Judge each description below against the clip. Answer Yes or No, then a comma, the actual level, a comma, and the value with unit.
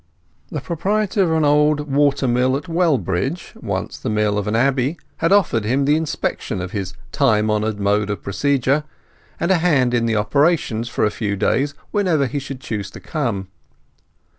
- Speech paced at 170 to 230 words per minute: Yes, average, 175 wpm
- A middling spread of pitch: No, wide, 6.1 semitones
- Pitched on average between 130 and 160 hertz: Yes, low, 135 Hz